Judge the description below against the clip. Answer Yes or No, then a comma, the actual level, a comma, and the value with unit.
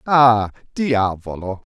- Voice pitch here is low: Yes, low, 115 Hz